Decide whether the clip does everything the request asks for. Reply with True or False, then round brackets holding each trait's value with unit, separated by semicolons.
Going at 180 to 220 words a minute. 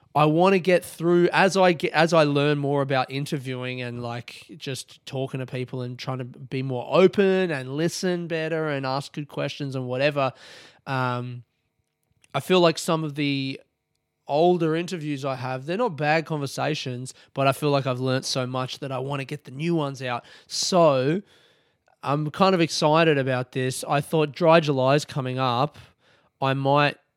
True (185 wpm)